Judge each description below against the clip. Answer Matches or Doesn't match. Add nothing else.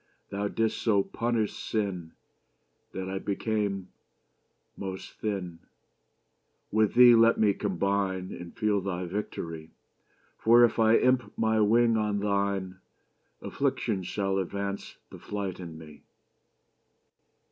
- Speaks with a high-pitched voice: Doesn't match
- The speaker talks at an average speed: Doesn't match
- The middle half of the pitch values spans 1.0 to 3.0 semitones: Matches